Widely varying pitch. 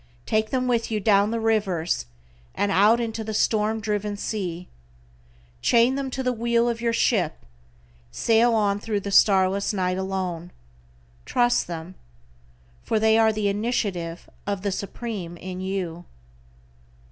No: average, 3.3 semitones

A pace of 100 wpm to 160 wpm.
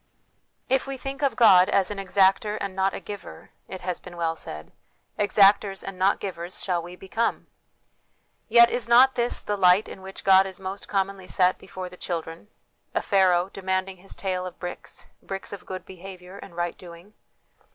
No: average, 190 wpm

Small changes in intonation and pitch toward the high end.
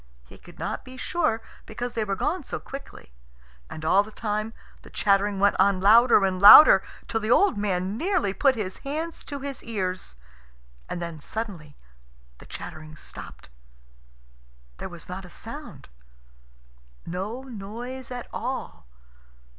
No: average, 5.0 semitones; high, 215 Hz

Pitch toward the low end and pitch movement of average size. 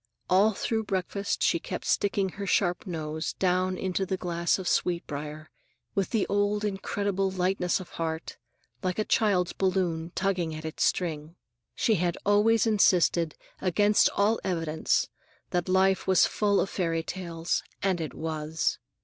No: medium, 185 Hz; average, 3.0 semitones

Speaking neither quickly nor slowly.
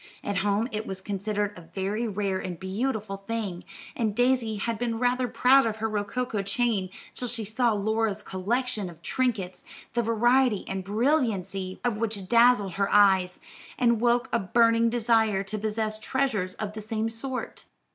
Yes: average, 165 wpm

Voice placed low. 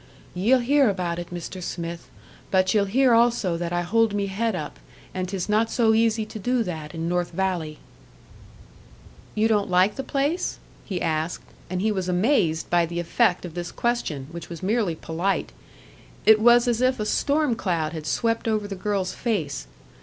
No: high, 195 Hz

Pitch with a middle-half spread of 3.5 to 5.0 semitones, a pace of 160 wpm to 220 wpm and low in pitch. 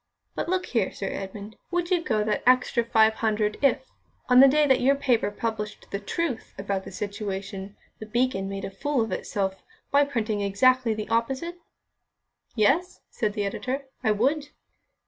No: average, 4.7 semitones; average, 170 wpm; high, 225 Hz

